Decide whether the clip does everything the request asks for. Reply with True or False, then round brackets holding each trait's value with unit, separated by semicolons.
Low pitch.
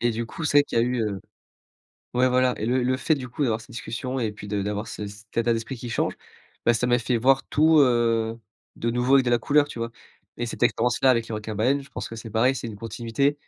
True (120 Hz)